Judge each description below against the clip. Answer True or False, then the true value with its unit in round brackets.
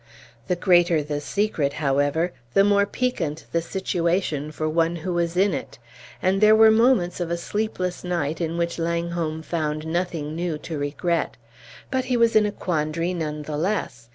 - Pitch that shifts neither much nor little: True (3.2 semitones)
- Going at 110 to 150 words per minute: False (175 wpm)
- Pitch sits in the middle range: True (170 Hz)